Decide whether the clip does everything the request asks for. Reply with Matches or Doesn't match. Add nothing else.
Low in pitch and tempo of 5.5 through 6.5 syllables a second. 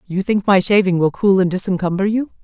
Doesn't match